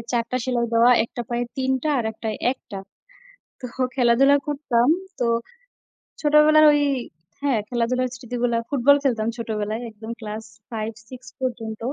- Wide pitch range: No, average, 2.7 semitones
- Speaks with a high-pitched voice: Yes, high, 240 Hz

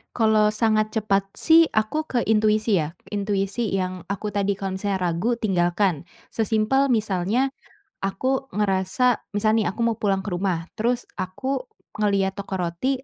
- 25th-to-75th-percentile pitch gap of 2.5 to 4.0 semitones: Yes, average, 2.9 semitones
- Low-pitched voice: No, high, 210 Hz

